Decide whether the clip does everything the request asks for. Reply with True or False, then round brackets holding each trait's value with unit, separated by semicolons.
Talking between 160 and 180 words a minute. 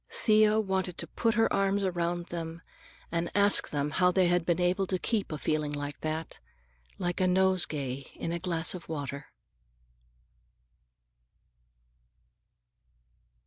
False (135 wpm)